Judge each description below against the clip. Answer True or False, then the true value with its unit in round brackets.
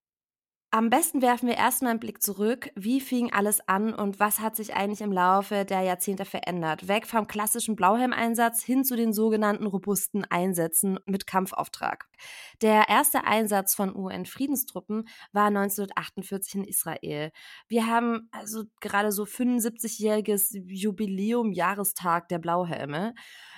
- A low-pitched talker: False (210 Hz)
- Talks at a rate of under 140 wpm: True (130 wpm)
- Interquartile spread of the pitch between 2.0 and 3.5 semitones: True (2.8 semitones)